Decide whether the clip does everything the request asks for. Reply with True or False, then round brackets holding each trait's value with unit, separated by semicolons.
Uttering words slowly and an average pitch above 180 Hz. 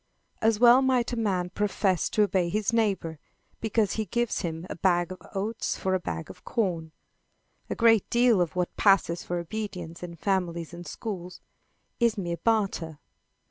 False (170 wpm; 190 Hz)